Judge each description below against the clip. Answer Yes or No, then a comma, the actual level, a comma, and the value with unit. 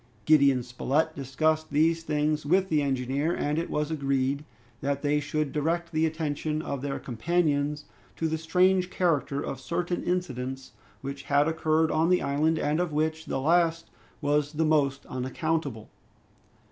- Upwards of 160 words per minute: No, average, 155 wpm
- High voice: No, medium, 150 Hz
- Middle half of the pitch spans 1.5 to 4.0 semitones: Yes, narrow, 2.5 semitones